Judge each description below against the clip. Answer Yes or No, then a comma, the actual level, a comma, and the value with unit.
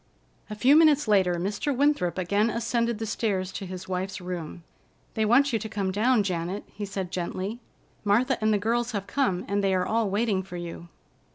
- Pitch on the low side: No, high, 205 Hz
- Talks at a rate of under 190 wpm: No, average, 195 wpm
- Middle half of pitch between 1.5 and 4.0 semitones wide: Yes, average, 3.7 semitones